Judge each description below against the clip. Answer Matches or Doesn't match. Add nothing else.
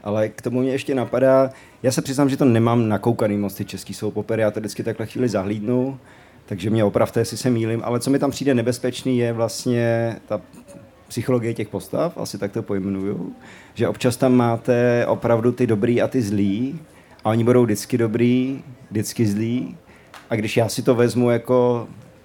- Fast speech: Matches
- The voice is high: Doesn't match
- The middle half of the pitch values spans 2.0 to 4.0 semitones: Matches